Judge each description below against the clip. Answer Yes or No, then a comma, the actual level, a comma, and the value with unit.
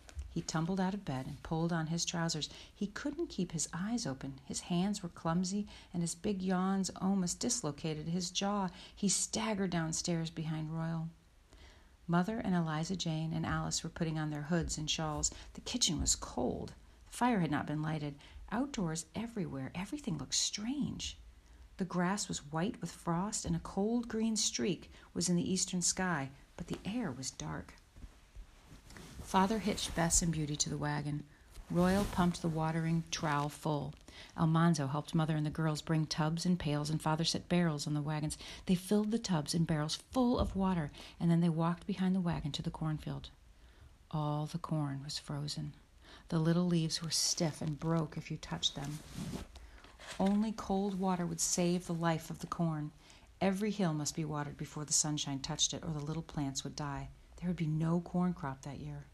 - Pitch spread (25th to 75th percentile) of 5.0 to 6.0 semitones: No, average, 3.5 semitones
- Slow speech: No, average, 185 wpm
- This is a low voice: No, medium, 165 Hz